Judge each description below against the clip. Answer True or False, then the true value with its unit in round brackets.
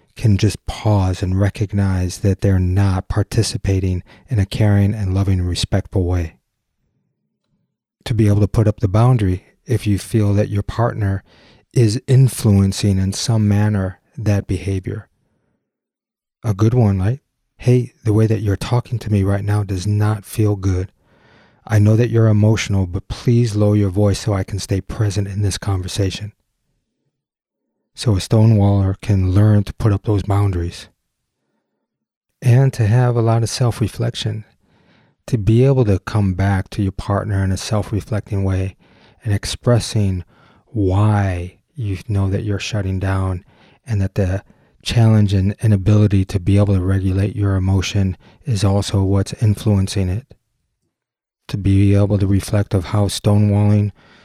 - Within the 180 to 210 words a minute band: False (155 wpm)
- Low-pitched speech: True (105 Hz)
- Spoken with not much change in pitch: True (2.1 semitones)